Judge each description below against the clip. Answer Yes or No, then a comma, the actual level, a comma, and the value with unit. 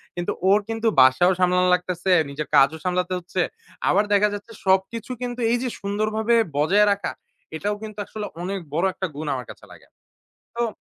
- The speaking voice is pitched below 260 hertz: Yes, high, 190 Hz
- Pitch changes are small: No, average, 3.1 semitones